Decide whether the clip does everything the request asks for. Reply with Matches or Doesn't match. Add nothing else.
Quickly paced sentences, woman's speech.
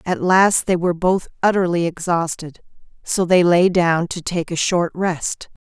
Doesn't match